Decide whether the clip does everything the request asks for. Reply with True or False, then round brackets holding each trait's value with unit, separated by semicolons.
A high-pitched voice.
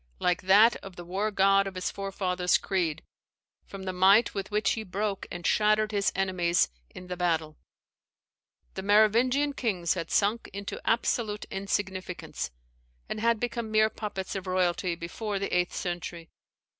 True (195 Hz)